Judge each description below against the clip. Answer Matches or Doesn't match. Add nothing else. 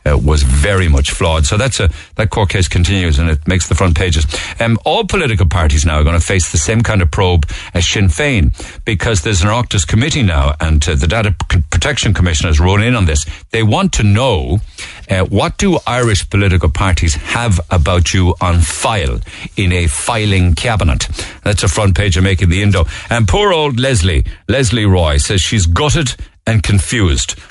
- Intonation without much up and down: Doesn't match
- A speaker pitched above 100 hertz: Doesn't match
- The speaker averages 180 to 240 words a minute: Matches